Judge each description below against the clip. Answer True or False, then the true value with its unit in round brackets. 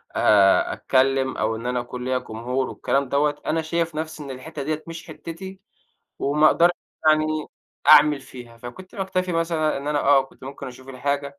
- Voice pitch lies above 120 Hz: True (140 Hz)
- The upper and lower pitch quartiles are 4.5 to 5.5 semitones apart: False (3.3 semitones)